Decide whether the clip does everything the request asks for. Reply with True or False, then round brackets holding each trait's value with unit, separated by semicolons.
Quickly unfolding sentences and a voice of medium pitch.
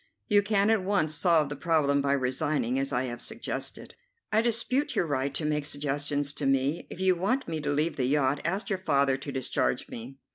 True (210 wpm; 145 Hz)